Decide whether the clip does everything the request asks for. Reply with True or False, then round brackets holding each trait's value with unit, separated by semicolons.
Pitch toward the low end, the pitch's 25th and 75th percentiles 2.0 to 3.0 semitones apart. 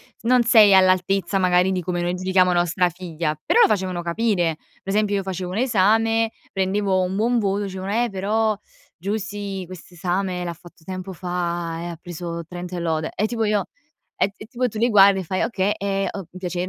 False (190 Hz; 2.6 semitones)